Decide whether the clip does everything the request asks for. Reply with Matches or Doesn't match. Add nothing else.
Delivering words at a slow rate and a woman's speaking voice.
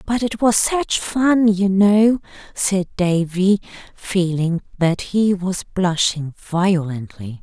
Matches